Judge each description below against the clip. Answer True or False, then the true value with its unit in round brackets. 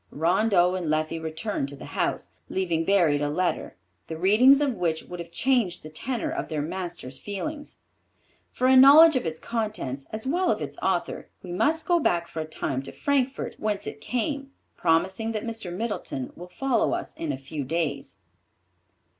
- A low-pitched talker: False (185 Hz)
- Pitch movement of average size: False (7.6 semitones)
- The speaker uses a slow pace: False (180 wpm)